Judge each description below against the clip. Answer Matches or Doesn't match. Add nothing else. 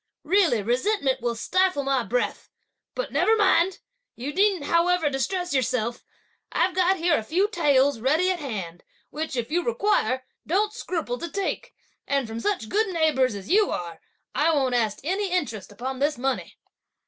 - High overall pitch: Matches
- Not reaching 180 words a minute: Matches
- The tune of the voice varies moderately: Doesn't match